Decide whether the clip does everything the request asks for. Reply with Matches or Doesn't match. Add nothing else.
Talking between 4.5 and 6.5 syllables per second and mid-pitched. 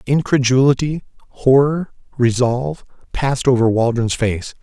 Doesn't match